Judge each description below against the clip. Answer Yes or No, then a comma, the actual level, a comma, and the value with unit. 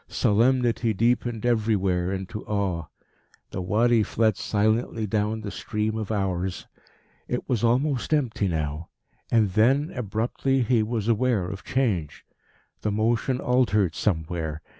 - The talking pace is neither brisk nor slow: No, slow, 125 wpm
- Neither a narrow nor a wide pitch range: Yes, average, 3.8 semitones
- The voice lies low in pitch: Yes, low, 110 Hz